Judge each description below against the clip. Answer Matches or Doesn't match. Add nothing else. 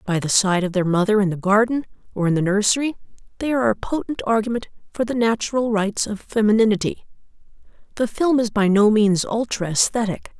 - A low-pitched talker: Doesn't match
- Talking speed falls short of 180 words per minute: Doesn't match